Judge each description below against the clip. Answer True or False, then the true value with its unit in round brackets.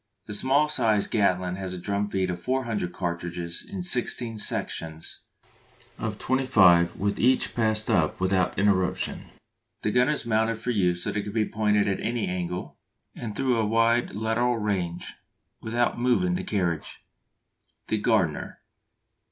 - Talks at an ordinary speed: True (150 wpm)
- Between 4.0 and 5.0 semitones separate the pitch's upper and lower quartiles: True (4.4 semitones)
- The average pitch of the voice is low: True (105 Hz)